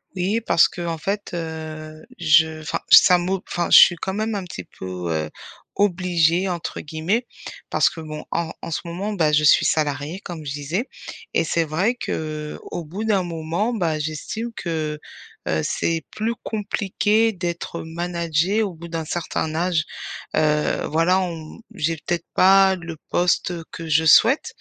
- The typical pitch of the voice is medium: Yes, medium, 170 Hz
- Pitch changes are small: No, average, 3.2 semitones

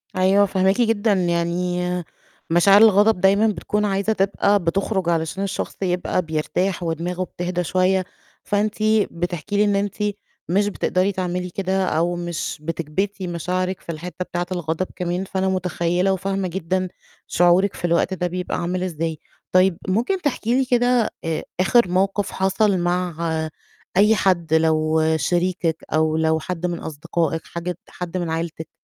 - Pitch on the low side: No, medium, 180 Hz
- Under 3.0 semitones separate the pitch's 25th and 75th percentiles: Yes, narrow, 2.4 semitones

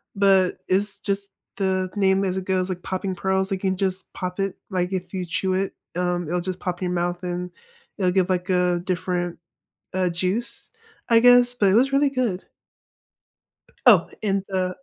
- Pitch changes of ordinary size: No, narrow, 1.5 semitones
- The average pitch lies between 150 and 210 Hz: Yes, medium, 185 Hz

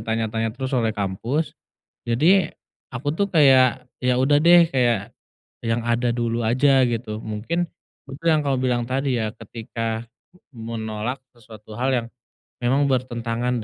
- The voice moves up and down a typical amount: Yes, average, 3.0 semitones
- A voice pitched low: Yes, low, 120 Hz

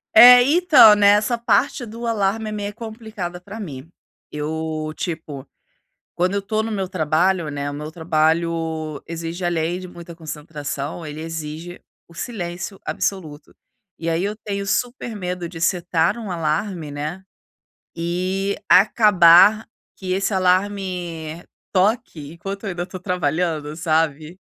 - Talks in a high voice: No, medium, 175 Hz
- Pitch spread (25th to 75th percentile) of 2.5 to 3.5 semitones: No, average, 3.9 semitones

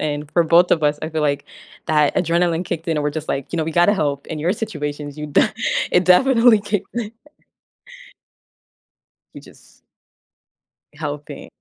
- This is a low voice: No, medium, 160 Hz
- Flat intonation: No, average, 3.2 semitones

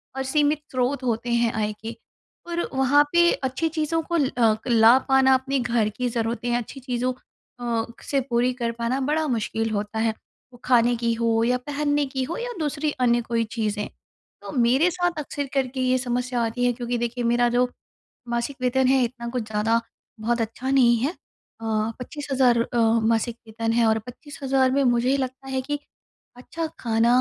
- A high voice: Yes, high, 245 Hz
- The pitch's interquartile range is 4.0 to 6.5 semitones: No, narrow, 2.5 semitones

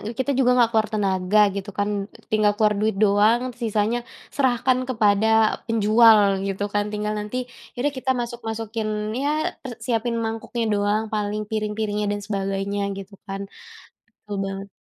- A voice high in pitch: Yes, high, 215 Hz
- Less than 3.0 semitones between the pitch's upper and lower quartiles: Yes, narrow, 2.4 semitones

